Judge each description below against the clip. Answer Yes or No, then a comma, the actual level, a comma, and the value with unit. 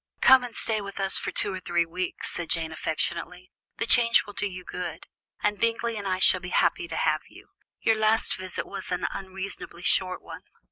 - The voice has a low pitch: No, high, 190 Hz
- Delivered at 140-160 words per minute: No, fast, 205 wpm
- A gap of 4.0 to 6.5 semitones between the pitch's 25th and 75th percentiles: No, average, 3.3 semitones